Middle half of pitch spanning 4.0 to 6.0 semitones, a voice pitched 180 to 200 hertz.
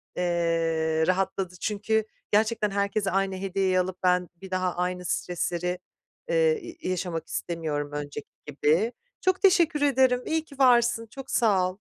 Yes: average, 4.9 semitones; high, 190 Hz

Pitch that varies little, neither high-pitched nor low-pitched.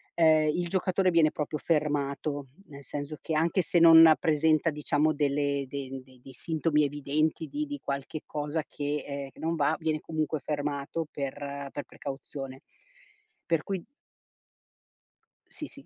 Yes: narrow, 2.3 semitones; medium, 150 Hz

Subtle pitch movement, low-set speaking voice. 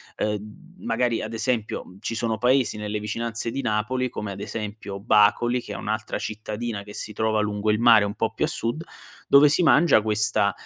Yes: narrow, 2.2 semitones; low, 110 Hz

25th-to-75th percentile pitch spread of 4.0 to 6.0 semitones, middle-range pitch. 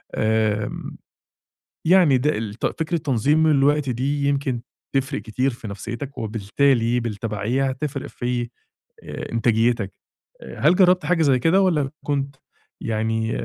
No: average, 4.4 semitones; low, 130 Hz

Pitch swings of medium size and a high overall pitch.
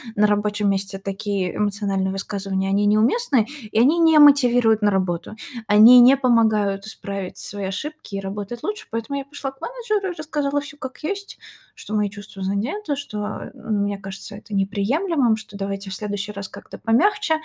No: wide, 5.9 semitones; high, 215 Hz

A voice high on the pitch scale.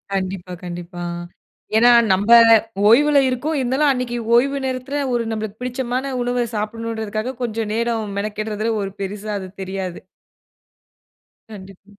Yes: high, 225 Hz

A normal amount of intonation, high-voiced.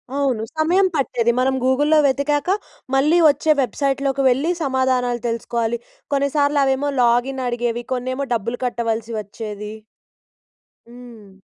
Yes: average, 3.0 semitones; very high, 255 Hz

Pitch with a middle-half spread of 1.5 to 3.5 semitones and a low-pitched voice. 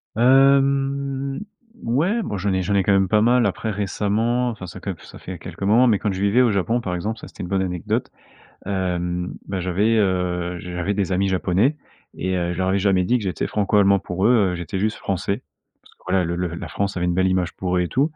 No: average, 3.9 semitones; low, 100 Hz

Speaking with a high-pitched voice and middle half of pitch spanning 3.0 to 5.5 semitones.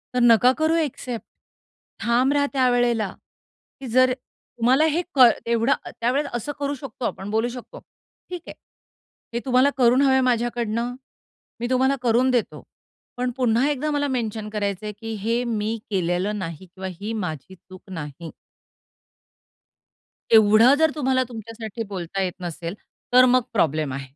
Yes: high, 235 Hz; average, 3.8 semitones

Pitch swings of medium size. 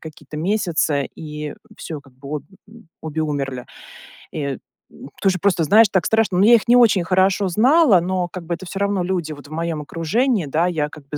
Yes: average, 4.6 semitones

